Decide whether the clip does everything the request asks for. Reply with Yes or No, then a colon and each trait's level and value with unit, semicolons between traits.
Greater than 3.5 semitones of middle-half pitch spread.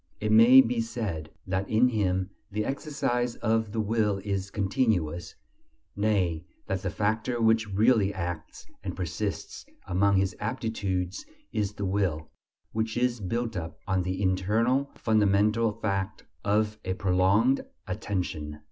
No: average, 3.2 semitones